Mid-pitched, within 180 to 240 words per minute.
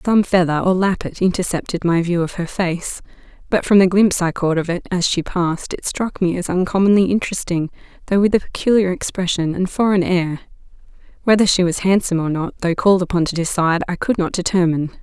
Yes: medium, 180 Hz; average, 195 wpm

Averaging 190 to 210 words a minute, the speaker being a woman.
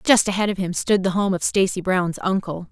No: fast, 245 wpm; female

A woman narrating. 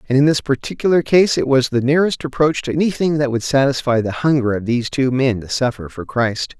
No: male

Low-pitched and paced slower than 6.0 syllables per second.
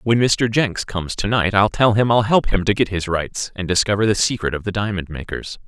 Yes: low, 105 Hz; 5.5 syllables/s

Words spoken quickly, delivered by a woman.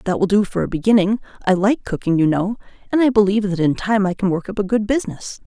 Yes: fast, 260 wpm; female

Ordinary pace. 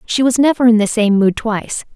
No: fast, 245 wpm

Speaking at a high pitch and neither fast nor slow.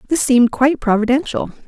Yes: very high, 260 Hz; average, 145 wpm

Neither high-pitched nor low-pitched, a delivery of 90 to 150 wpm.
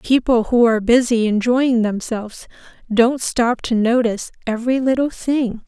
No: high, 235 Hz; average, 140 wpm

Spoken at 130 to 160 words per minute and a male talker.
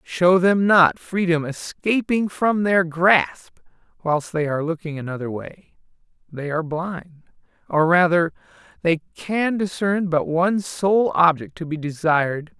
Yes: average, 150 wpm; male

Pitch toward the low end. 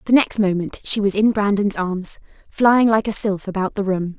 No: high, 200 Hz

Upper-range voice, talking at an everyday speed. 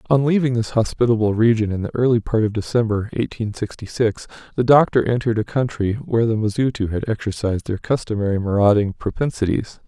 No: low, 110 Hz; average, 170 wpm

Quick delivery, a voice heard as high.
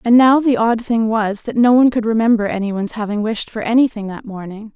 Yes: fast, 225 wpm; high, 225 Hz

